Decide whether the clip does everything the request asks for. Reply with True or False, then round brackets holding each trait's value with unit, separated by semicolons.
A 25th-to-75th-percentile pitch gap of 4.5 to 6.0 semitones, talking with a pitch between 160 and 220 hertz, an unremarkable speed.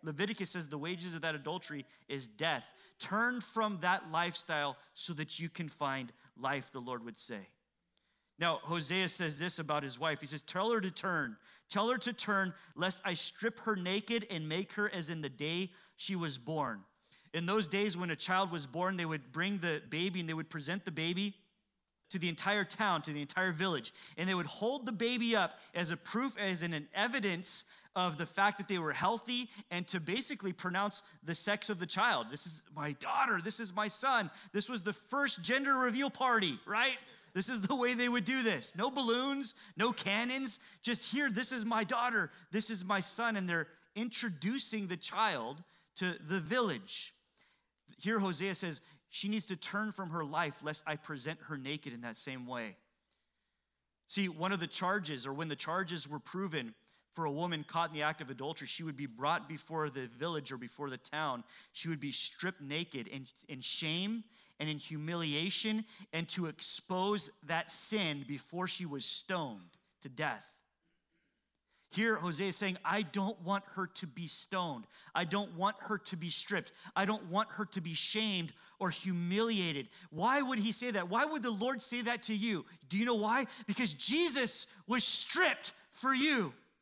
True (5.2 semitones; 185 Hz; 195 wpm)